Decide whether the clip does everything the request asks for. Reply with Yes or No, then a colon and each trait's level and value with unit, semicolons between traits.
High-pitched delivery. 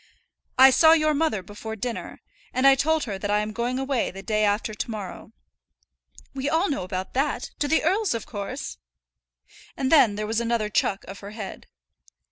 Yes: high, 235 Hz